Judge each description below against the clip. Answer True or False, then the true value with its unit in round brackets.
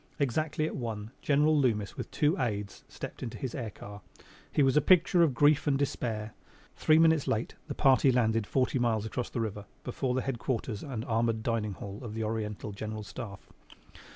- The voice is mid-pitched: False (120 Hz)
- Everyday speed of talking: True (185 wpm)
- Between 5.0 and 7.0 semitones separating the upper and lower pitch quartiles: False (4.2 semitones)